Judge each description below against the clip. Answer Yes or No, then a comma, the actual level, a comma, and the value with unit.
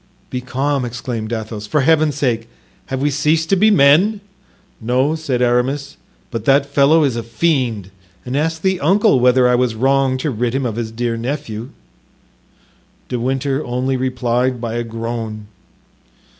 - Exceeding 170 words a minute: No, average, 160 wpm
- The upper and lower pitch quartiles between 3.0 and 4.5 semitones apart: Yes, average, 3.4 semitones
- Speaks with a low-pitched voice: Yes, low, 130 Hz